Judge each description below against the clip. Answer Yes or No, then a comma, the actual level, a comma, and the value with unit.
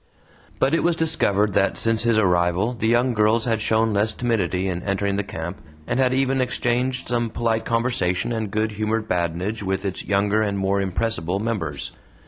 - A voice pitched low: Yes, low, 110 Hz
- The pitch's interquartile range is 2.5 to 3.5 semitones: Yes, average, 3.2 semitones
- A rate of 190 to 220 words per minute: No, average, 180 wpm